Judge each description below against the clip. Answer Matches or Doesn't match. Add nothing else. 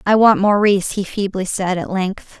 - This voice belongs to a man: Doesn't match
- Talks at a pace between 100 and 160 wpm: Doesn't match